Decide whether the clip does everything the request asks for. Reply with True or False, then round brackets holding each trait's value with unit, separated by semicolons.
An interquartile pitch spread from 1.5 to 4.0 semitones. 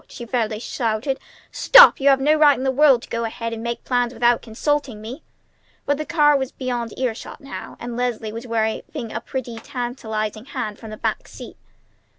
True (3.1 semitones)